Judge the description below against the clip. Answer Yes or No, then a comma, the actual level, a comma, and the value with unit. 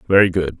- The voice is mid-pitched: No, very low, 85 Hz